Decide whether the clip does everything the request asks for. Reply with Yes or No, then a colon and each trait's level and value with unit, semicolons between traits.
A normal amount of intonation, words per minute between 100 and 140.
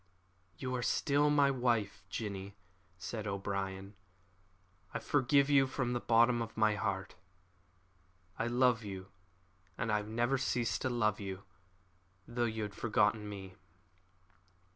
Yes: average, 3.7 semitones; slow, 135 wpm